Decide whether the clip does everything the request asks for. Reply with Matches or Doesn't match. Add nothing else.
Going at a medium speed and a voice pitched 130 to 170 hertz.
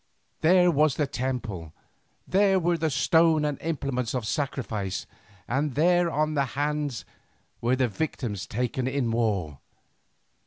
Doesn't match